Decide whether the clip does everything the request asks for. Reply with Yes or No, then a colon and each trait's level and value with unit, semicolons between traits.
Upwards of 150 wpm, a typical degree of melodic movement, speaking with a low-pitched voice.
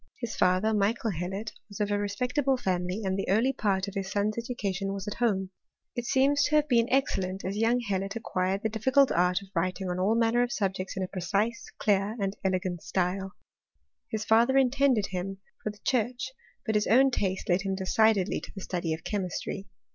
No: average, 185 wpm; average, 3.6 semitones; high, 205 Hz